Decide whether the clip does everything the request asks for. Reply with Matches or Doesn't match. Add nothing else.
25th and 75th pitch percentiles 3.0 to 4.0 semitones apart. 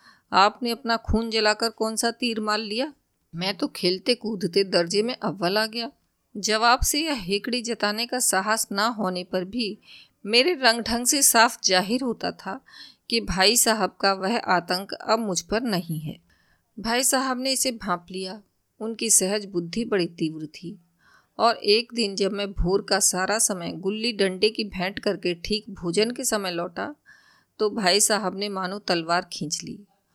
Matches